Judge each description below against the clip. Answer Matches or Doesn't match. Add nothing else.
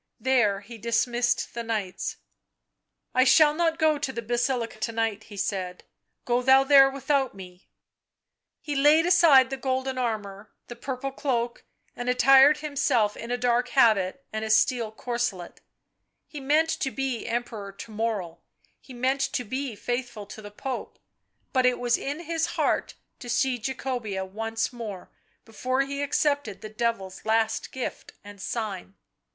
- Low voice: Doesn't match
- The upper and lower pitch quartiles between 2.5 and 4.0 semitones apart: Matches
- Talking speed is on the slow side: Doesn't match